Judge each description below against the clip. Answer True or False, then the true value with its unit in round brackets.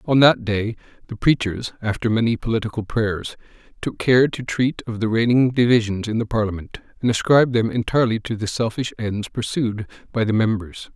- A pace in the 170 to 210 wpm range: True (175 wpm)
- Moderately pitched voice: False (115 Hz)